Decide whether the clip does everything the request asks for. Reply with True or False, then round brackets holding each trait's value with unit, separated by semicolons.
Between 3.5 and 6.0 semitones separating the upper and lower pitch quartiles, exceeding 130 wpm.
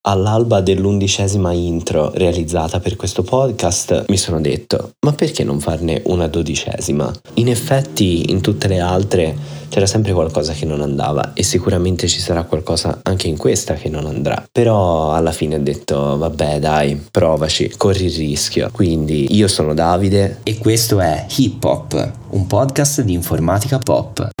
True (4.7 semitones; 155 wpm)